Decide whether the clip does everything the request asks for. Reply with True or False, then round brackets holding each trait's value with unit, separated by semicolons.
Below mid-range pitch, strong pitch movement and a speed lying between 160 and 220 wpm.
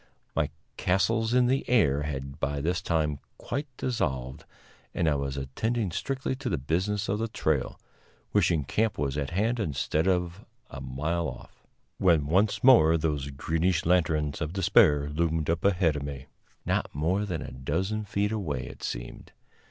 True (80 Hz; 5.8 semitones; 165 wpm)